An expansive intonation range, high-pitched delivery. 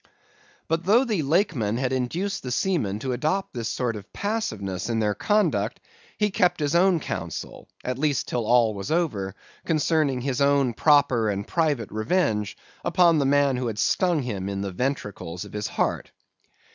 No: wide, 7.3 semitones; low, 130 Hz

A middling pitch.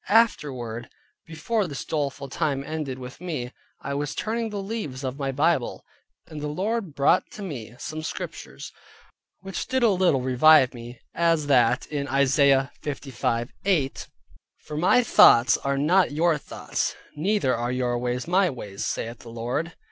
Yes: medium, 145 Hz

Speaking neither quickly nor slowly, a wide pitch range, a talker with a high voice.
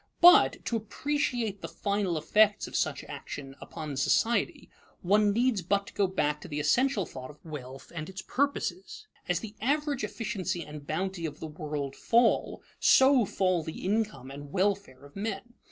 Yes: average, 170 wpm; wide, 6.9 semitones; high, 195 Hz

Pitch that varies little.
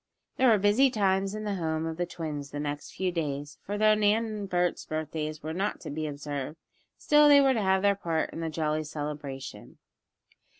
No: average, 5.3 semitones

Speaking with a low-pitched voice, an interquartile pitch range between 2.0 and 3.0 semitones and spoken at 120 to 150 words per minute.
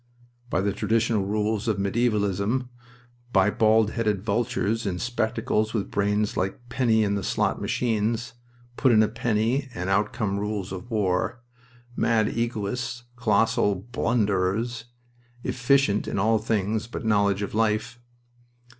Yes: low, 110 Hz; narrow, 2.5 semitones; slow, 135 wpm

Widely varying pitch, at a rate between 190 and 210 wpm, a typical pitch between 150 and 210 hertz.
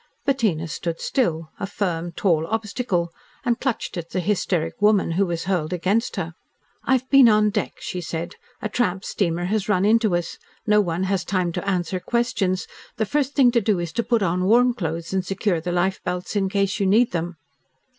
No: average, 3.8 semitones; average, 195 wpm; high, 190 Hz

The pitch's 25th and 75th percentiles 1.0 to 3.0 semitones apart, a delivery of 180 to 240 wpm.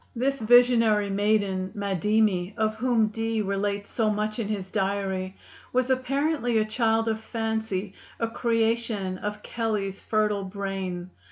No: narrow, 2.4 semitones; slow, 135 wpm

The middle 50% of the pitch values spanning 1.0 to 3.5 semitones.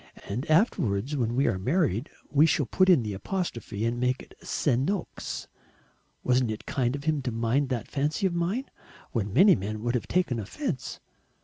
No: wide, 5.6 semitones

